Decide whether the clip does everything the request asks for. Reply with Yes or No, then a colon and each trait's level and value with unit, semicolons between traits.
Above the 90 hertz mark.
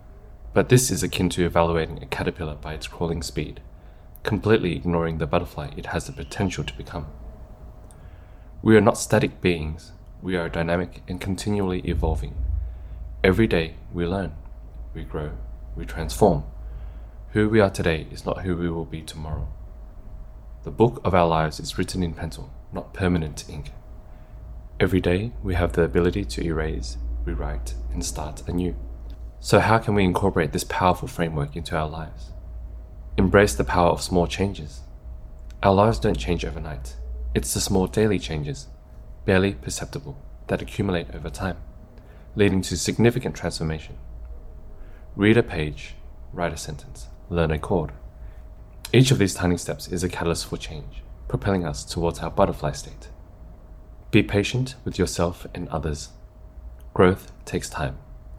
No: very low, 85 Hz